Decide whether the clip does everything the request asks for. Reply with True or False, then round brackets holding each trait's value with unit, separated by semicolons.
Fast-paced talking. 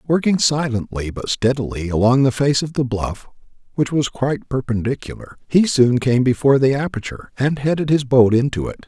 False (175 wpm)